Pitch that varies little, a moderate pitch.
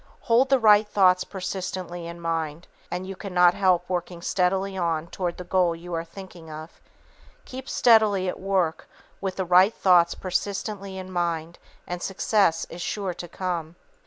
Yes: narrow, 2.2 semitones; medium, 180 Hz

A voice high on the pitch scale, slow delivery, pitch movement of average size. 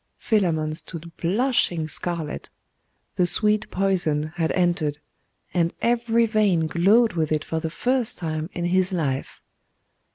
No: medium, 175 Hz; slow, 130 wpm; average, 4.8 semitones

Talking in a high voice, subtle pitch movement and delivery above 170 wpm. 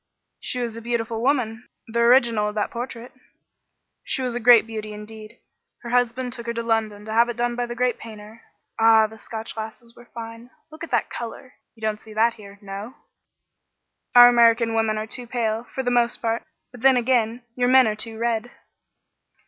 Yes: high, 230 Hz; narrow, 1.7 semitones; average, 195 wpm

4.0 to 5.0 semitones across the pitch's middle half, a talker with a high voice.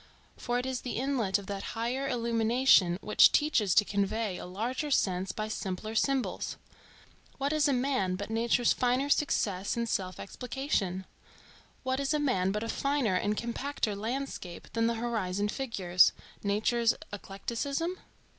Yes: average, 4.7 semitones; high, 230 Hz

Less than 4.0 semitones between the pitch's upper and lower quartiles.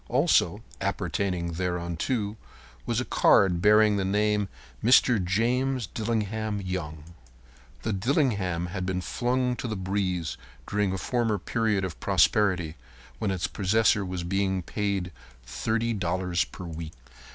Yes: average, 3.3 semitones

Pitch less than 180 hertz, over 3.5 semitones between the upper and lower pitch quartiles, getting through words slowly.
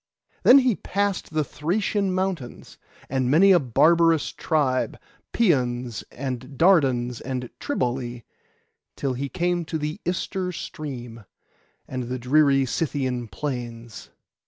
Yes: medium, 140 Hz; wide, 5.5 semitones; slow, 115 wpm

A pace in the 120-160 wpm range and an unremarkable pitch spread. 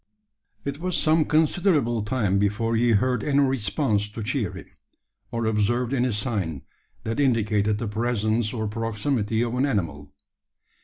Yes: average, 145 wpm; average, 3.8 semitones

